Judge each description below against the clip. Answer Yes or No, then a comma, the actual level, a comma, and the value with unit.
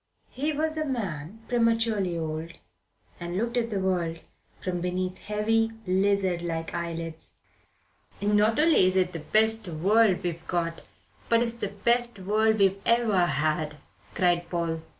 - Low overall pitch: No, high, 190 Hz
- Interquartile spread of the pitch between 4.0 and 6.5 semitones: Yes, average, 4.7 semitones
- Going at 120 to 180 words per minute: Yes, average, 145 wpm